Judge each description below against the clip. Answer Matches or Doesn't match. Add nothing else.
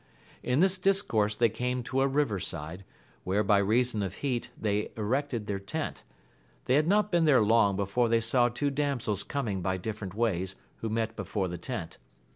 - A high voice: Doesn't match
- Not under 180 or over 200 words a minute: Matches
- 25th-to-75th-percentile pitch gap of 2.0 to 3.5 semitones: Doesn't match